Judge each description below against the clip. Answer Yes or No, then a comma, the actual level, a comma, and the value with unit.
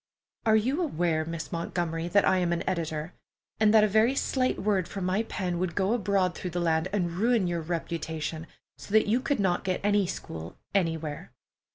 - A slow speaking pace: No, average, 195 wpm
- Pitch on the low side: No, medium, 180 Hz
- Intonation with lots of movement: No, average, 3.8 semitones